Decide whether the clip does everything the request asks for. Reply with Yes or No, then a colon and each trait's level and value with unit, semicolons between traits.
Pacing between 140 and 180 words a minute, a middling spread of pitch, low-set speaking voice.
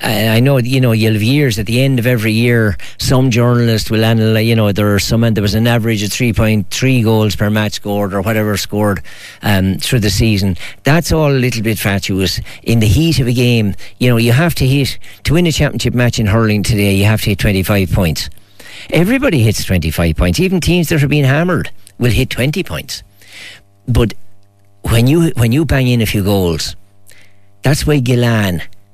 No: fast, 205 wpm; average, 3.7 semitones; low, 110 Hz